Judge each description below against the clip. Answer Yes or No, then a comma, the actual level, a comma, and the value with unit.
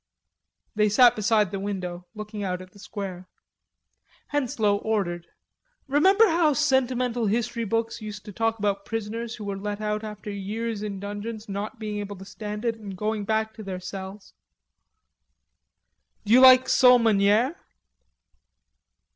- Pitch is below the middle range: No, high, 215 Hz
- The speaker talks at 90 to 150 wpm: Yes, average, 145 wpm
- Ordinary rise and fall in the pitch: No, narrow, 2.3 semitones